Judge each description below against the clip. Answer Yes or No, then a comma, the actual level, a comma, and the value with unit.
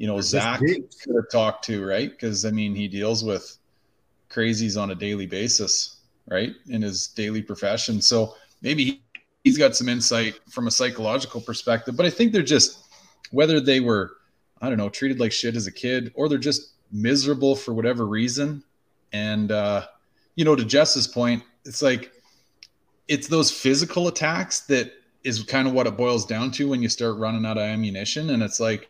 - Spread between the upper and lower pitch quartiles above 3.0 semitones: Yes, average, 4.1 semitones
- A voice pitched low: Yes, low, 115 Hz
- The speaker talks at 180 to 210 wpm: Yes, average, 190 wpm